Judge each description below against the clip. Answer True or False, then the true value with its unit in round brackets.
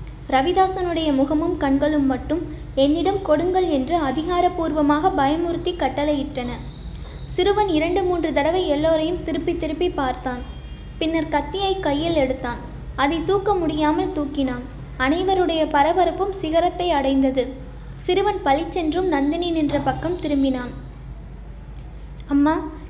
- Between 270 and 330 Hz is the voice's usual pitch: True (315 Hz)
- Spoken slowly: False (95 wpm)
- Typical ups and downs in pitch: True (3.8 semitones)